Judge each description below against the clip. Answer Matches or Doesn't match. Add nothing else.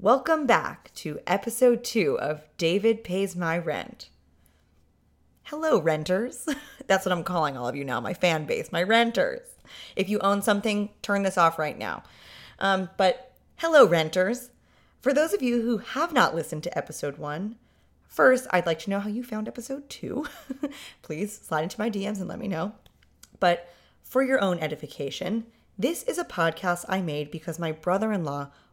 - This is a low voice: Doesn't match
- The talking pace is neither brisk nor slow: Matches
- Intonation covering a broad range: Matches